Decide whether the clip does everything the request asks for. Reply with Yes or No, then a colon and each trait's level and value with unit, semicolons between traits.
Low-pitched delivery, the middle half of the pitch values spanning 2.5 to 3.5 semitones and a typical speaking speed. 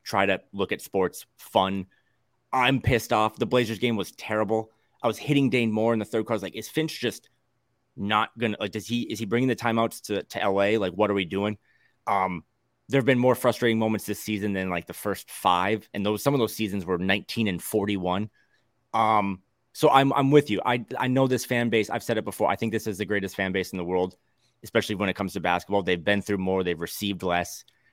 No: low, 110 Hz; average, 3.2 semitones; fast, 240 wpm